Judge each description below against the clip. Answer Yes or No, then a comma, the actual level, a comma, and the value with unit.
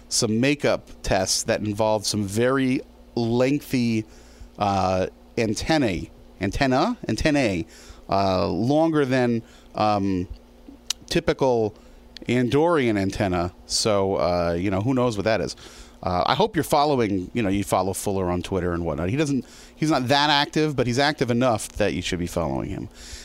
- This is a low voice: Yes, low, 105 Hz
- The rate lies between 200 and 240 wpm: No, average, 150 wpm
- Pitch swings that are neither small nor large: No, wide, 5.8 semitones